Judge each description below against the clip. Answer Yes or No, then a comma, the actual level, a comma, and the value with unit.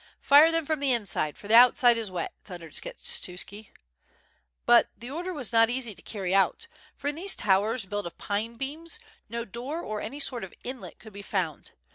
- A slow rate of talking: No, average, 200 wpm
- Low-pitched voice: No, high, 230 Hz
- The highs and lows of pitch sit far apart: Yes, wide, 5.8 semitones